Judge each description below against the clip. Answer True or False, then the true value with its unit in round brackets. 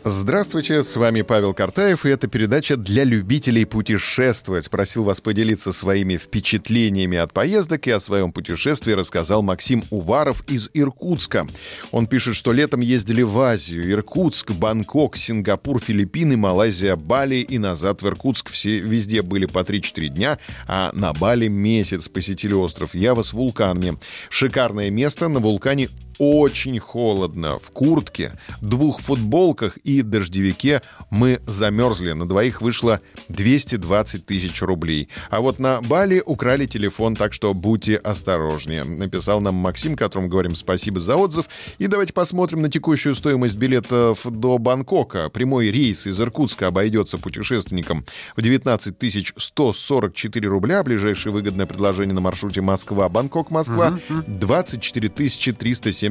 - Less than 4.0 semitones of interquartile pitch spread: False (5.0 semitones)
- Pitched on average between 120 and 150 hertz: False (110 Hz)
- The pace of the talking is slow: False (135 wpm)